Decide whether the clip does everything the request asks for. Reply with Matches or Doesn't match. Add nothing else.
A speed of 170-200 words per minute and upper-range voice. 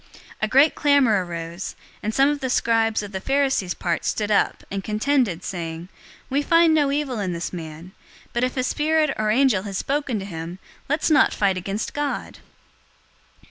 Matches